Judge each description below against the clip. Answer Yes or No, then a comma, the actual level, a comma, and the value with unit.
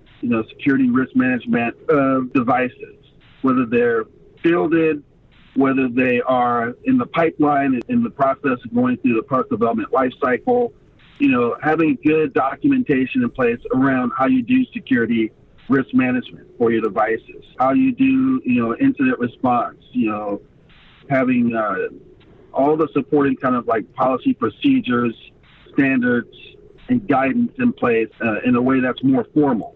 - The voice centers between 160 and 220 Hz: No, medium, 140 Hz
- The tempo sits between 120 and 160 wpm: Yes, average, 150 wpm